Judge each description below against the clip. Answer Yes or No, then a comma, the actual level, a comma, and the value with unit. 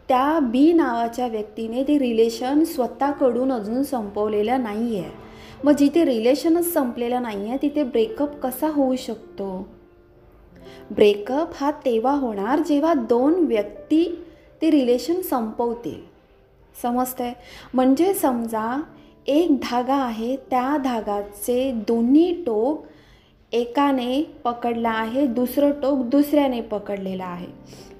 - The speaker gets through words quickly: No, average, 105 wpm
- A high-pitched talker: Yes, very high, 255 Hz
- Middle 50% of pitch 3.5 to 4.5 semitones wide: Yes, average, 3.9 semitones